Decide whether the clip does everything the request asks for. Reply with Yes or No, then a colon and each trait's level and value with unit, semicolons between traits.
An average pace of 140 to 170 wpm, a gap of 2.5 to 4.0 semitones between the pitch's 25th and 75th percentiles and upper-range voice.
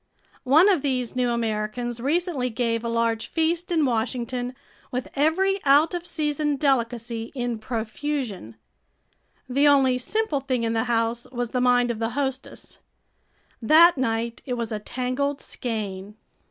Yes: average, 145 wpm; average, 3.7 semitones; very high, 250 Hz